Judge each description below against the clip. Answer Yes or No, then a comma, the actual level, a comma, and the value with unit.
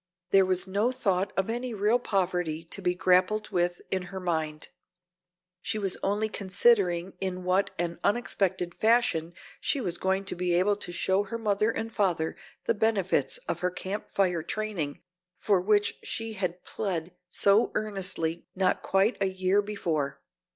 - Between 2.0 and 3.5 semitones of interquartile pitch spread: Yes, average, 2.8 semitones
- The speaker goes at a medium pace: Yes, average, 165 wpm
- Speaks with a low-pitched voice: No, high, 190 Hz